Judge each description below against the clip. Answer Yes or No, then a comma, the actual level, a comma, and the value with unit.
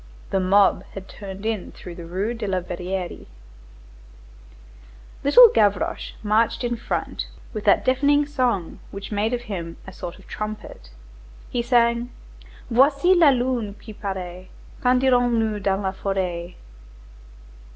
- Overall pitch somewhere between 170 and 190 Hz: No, high, 210 Hz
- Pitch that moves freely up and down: No, average, 4.2 semitones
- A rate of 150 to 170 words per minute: No, average, 140 wpm